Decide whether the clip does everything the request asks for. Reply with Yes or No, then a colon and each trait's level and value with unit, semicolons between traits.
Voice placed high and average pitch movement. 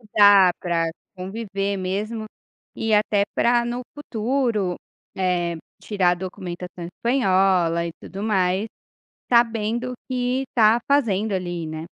Yes: high, 200 Hz; average, 4.1 semitones